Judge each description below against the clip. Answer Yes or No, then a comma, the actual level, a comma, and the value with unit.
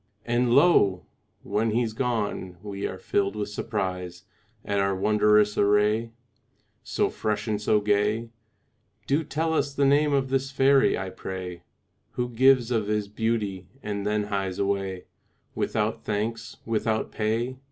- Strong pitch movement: No, average, 3.0 semitones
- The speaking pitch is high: No, low, 105 Hz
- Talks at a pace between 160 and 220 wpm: No, average, 140 wpm